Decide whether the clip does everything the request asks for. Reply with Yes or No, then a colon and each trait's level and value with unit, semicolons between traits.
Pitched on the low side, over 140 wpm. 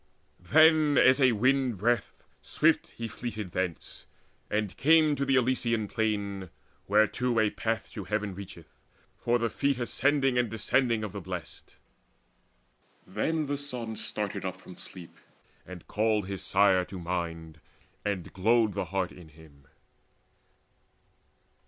No: low, 105 Hz; slow, 135 wpm